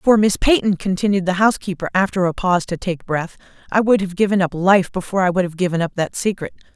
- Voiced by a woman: Yes, female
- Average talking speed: No, fast, 230 wpm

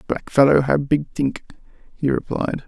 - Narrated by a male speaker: Yes, male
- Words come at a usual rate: Yes, average, 155 wpm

